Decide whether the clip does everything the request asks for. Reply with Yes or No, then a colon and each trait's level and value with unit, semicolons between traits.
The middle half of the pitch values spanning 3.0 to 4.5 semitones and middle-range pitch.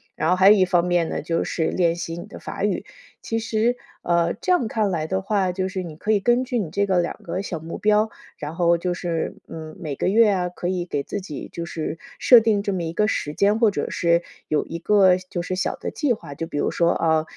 Yes: average, 3.6 semitones; medium, 180 Hz